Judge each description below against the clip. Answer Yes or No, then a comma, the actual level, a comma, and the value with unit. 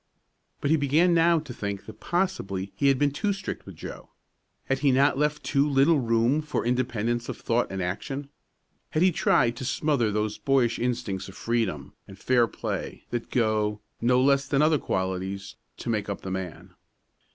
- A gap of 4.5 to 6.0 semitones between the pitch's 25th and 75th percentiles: Yes, wide, 5.4 semitones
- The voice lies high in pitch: No, low, 125 Hz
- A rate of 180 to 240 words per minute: Yes, average, 185 wpm